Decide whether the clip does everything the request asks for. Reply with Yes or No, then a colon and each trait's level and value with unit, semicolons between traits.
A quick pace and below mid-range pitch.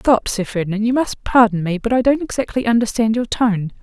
No: fast, 220 wpm; high, 225 Hz